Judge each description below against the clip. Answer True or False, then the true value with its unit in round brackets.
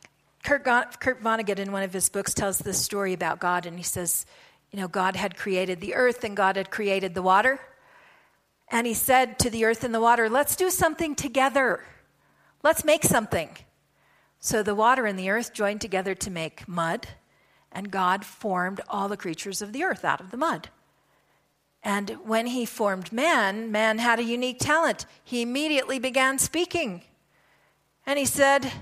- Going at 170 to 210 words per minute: True (180 wpm)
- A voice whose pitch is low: False (220 Hz)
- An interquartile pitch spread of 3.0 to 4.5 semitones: False (5.2 semitones)